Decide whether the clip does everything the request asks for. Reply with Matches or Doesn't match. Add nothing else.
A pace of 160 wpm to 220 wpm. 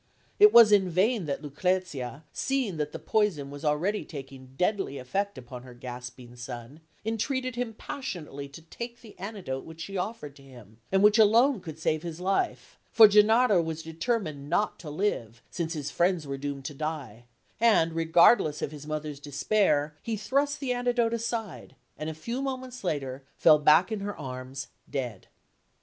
Matches